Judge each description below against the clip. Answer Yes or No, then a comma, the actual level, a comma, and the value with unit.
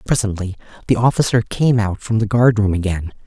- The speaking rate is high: No, average, 185 wpm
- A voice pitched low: Yes, low, 105 Hz